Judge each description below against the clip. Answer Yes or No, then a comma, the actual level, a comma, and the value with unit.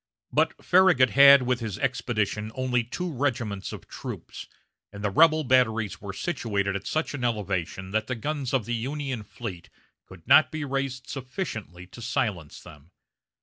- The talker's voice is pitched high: No, low, 120 Hz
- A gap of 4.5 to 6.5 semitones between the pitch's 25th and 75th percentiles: Yes, average, 5.2 semitones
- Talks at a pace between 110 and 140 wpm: No, average, 160 wpm